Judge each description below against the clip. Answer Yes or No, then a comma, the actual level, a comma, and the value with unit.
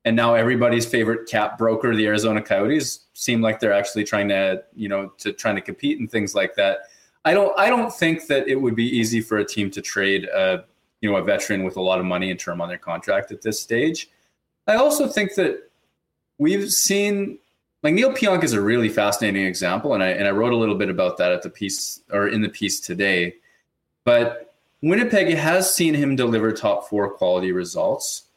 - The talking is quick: Yes, fast, 210 wpm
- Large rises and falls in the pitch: Yes, wide, 8.0 semitones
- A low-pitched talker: Yes, low, 115 Hz